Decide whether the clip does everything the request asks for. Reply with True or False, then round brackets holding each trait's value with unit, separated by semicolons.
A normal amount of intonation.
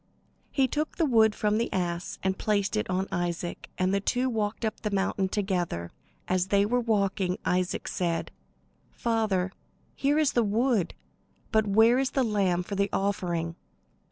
True (3.5 semitones)